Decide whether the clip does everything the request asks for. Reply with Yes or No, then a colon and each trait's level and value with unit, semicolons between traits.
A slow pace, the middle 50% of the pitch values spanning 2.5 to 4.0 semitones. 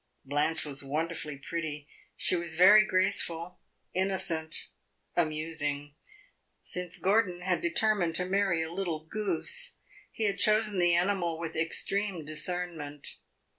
Yes: slow, 120 wpm; average, 3.3 semitones